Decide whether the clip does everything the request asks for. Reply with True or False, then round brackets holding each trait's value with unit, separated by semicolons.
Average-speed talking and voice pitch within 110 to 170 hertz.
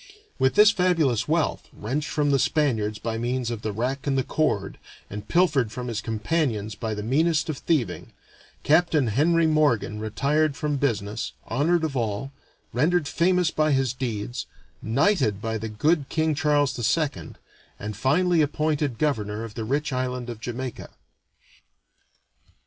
True (150 wpm; 135 Hz)